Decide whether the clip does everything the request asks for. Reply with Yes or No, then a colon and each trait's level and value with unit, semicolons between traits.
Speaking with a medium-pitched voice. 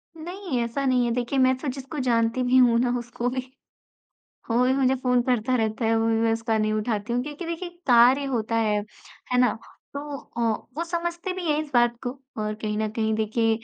No: high, 245 Hz